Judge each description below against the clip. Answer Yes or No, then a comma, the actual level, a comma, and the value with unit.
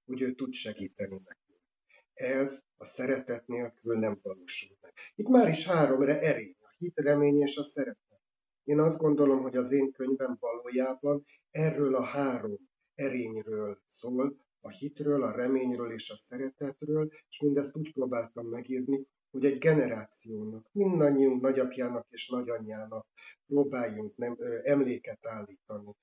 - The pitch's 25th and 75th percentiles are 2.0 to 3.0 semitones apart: No, average, 3.4 semitones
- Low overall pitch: Yes, low, 130 Hz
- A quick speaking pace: No, average, 140 wpm